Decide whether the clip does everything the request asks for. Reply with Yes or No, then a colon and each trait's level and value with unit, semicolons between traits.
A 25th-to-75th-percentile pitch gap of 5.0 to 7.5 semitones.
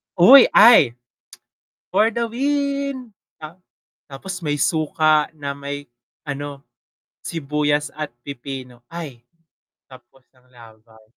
Yes: wide, 5.4 semitones